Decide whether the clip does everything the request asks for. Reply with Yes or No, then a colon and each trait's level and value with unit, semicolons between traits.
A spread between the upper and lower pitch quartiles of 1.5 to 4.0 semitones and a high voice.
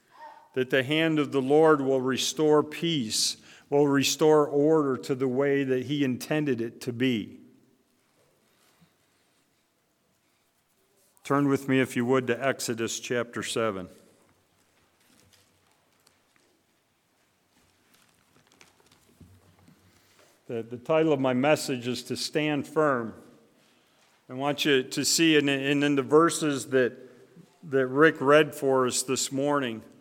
No: average, 2.9 semitones; low, 135 Hz